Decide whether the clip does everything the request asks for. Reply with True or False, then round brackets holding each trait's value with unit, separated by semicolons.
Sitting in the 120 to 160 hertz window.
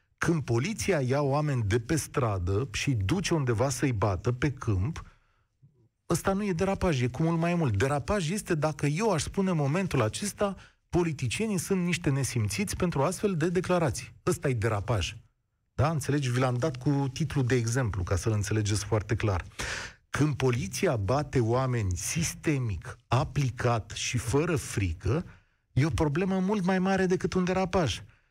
True (135 Hz)